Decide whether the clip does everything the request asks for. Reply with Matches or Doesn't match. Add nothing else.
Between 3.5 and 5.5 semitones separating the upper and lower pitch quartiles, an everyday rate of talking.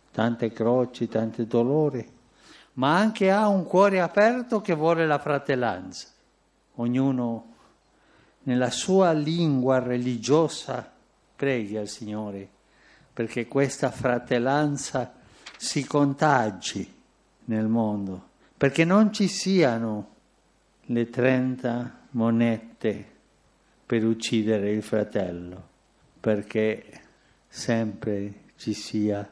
Doesn't match